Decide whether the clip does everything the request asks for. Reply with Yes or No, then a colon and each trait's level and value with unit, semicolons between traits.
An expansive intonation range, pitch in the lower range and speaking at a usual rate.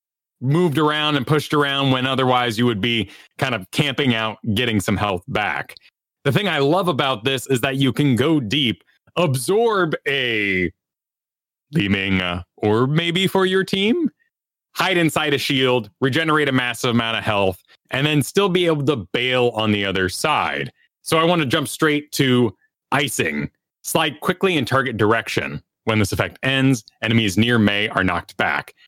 Yes: wide, 5.8 semitones; low, 130 Hz; average, 170 wpm